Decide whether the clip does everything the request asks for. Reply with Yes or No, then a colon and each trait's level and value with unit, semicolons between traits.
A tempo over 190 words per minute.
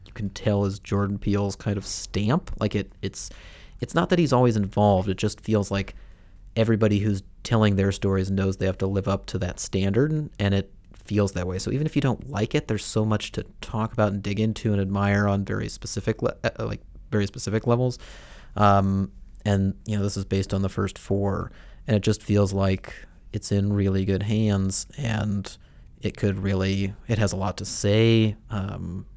Yes: average, 200 wpm